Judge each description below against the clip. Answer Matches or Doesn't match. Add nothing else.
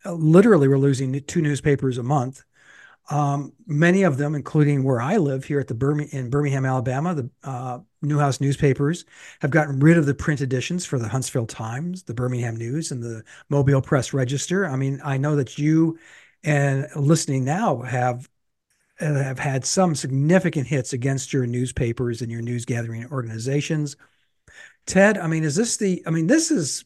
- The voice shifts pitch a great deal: Doesn't match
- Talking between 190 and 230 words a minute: Doesn't match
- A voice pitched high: Doesn't match